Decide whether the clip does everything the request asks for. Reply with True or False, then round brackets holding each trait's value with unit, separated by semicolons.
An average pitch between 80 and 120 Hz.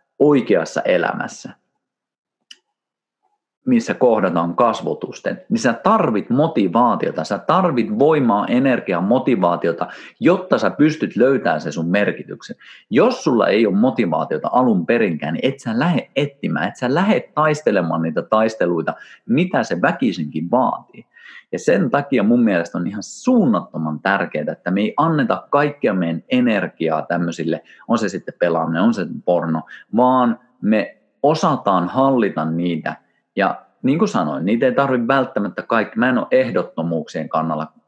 False (130 Hz)